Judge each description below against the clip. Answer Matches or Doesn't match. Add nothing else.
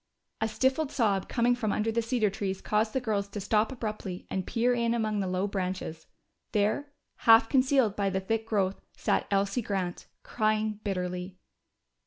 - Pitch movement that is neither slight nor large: Matches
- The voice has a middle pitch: Doesn't match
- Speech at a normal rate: Matches